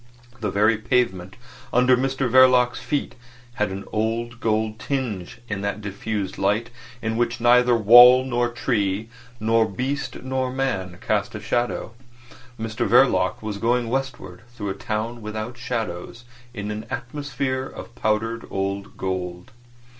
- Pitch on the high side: No, low, 115 Hz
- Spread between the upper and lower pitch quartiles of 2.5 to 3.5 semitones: Yes, average, 3.0 semitones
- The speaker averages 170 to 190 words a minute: No, average, 140 wpm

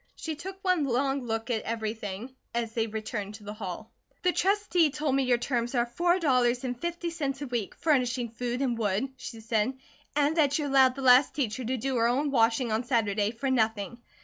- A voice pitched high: Yes, very high, 250 Hz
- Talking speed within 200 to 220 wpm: Yes, fast, 205 wpm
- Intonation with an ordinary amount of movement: Yes, average, 3.7 semitones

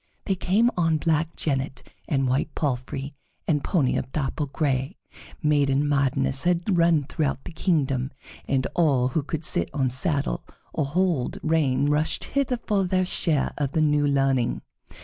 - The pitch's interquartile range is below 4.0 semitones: Yes, average, 3.4 semitones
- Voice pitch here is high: No, medium, 145 Hz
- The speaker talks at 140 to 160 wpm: Yes, average, 155 wpm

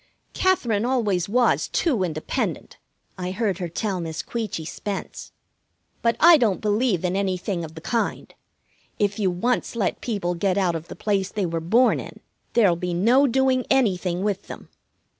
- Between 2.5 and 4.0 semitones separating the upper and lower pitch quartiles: No, average, 4.7 semitones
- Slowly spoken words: No, average, 165 wpm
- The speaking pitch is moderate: No, high, 200 Hz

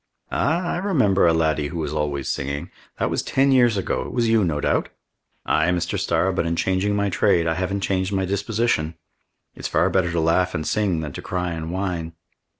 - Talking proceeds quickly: Yes, fast, 210 wpm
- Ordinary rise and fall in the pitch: Yes, average, 3.8 semitones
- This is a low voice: Yes, very low, 90 Hz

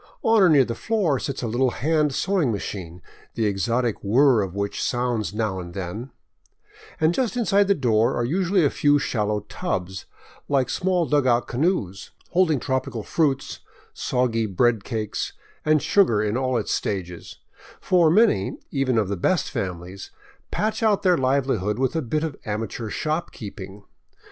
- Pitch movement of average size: No, wide, 6.9 semitones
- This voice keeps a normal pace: Yes, average, 160 wpm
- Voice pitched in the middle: No, low, 125 Hz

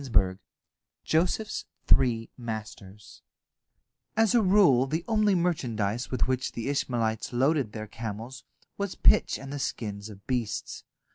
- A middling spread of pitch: No, wide, 6.5 semitones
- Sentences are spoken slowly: Yes, slow, 125 wpm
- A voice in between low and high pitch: No, low, 125 Hz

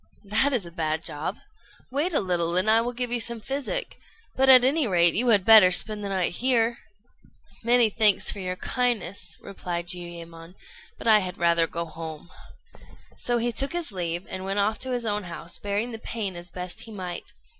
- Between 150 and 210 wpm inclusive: Yes, average, 200 wpm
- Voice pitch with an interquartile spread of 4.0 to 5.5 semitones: Yes, average, 5.2 semitones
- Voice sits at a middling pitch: No, high, 200 Hz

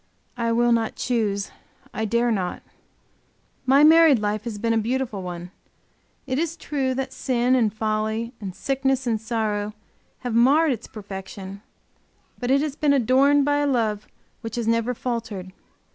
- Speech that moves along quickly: No, average, 160 wpm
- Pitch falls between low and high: No, high, 235 Hz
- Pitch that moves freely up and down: No, average, 3.7 semitones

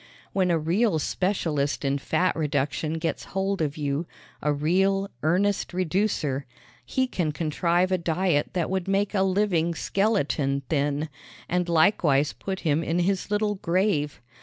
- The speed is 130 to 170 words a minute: Yes, average, 145 wpm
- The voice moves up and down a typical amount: Yes, average, 4.4 semitones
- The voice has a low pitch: No, medium, 170 Hz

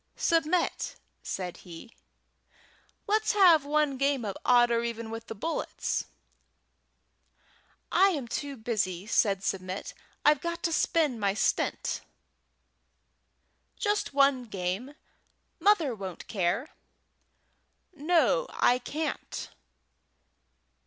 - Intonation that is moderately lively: No, wide, 7.2 semitones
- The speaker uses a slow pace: Yes, slow, 100 wpm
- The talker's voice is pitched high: Yes, very high, 255 Hz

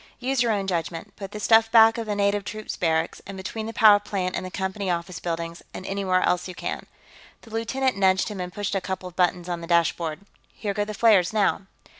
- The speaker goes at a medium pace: No, fast, 230 wpm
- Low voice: No, high, 195 Hz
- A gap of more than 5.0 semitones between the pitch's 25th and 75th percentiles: No, average, 3.1 semitones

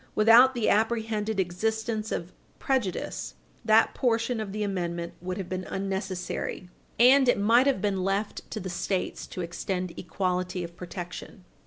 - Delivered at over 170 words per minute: No, average, 150 wpm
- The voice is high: Yes, high, 200 Hz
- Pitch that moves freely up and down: No, average, 3.5 semitones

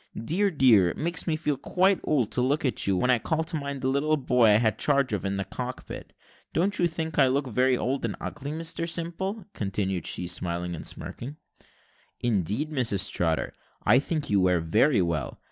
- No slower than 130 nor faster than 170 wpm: No, fast, 205 wpm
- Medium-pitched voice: No, low, 130 Hz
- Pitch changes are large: Yes, wide, 7.4 semitones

